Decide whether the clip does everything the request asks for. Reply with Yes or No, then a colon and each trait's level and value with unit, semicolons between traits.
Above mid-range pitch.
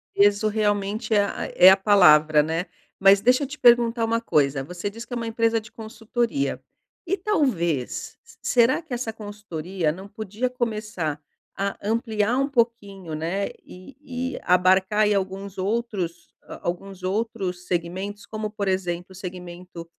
Yes: high, 205 Hz